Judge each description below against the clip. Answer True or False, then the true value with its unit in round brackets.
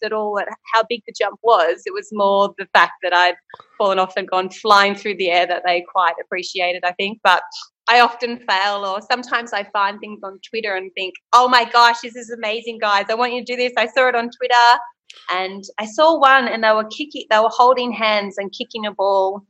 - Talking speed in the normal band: False (235 wpm)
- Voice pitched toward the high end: True (215 Hz)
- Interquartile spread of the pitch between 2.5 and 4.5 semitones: True (3.7 semitones)